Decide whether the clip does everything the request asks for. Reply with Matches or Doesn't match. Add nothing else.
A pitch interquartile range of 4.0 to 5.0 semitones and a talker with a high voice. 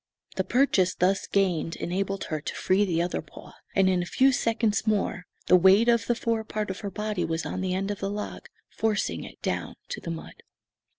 Doesn't match